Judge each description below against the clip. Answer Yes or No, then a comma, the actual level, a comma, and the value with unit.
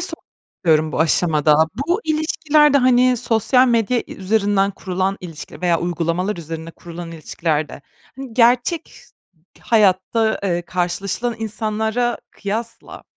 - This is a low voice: No, high, 200 Hz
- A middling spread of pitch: No, wide, 5.7 semitones